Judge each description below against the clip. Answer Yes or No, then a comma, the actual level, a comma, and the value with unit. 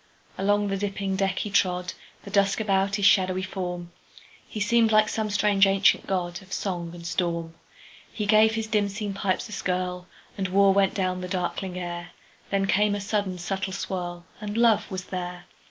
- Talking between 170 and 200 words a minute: No, average, 155 wpm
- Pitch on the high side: Yes, high, 195 Hz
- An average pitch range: No, narrow, 2.1 semitones